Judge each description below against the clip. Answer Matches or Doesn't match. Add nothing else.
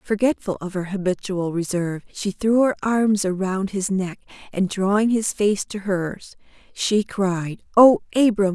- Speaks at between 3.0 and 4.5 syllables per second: Matches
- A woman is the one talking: Matches